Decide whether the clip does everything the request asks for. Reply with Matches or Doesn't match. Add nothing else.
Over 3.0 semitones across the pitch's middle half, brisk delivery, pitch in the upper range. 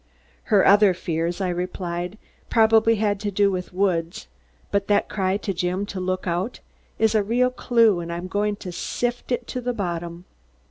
Doesn't match